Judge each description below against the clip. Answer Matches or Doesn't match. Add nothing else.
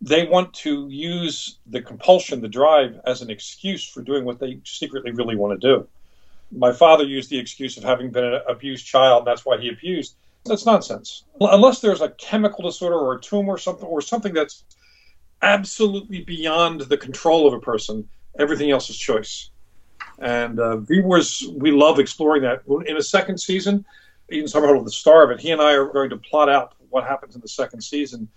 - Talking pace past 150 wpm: Matches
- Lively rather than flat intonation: Matches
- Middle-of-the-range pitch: Matches